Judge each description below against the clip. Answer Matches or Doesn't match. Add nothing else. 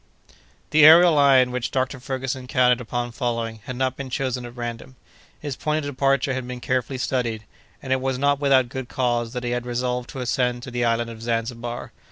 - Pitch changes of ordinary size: Doesn't match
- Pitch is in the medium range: Doesn't match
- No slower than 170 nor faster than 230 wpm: Matches